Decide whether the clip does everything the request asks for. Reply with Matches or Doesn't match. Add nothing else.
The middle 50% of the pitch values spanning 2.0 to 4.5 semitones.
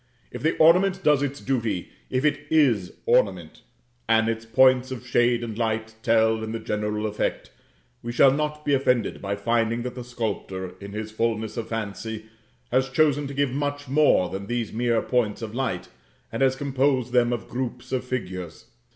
Matches